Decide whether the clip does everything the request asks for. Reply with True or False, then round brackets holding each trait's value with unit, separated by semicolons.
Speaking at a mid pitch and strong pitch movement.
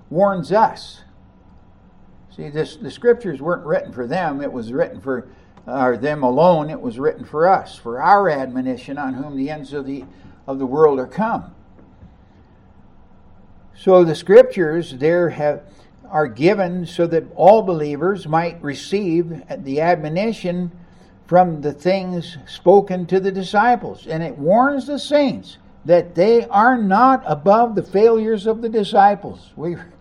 True (165 Hz; 6.7 semitones)